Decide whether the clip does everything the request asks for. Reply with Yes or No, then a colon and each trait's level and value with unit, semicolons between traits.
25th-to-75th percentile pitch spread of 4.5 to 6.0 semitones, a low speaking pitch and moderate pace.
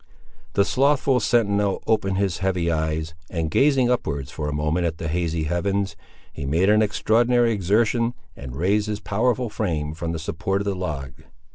Yes: average, 5.3 semitones; very low, 95 Hz; average, 170 wpm